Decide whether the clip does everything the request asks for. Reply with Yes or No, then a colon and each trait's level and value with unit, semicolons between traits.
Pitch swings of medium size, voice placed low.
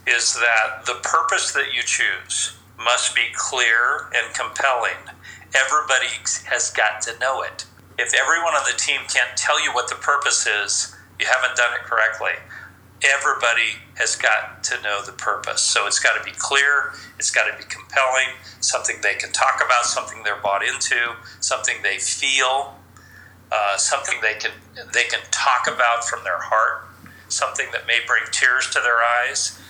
Yes: average, 3.9 semitones; low, 115 Hz